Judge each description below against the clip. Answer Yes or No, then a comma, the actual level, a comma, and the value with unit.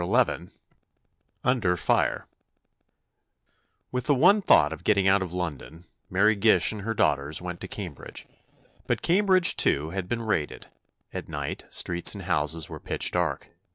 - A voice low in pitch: Yes, very low, 95 Hz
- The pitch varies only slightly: No, average, 5.2 semitones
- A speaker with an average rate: Yes, average, 150 wpm